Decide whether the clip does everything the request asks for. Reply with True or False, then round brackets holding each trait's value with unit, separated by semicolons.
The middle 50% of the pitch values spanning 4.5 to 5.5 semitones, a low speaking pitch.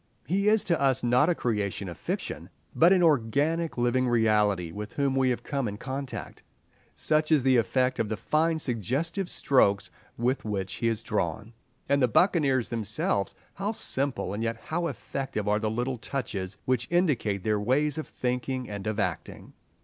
True (5.2 semitones; 125 Hz)